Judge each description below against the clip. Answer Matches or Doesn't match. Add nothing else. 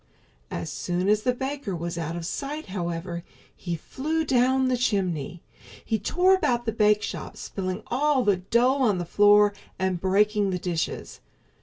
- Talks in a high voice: Matches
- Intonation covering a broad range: Matches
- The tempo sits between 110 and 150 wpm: Doesn't match